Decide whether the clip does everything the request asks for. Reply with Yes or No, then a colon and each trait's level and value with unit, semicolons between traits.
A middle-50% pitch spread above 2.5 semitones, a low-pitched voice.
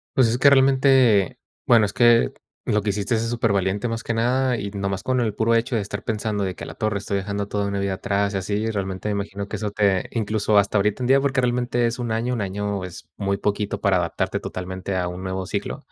Yes: average, 2.9 semitones; low, 105 Hz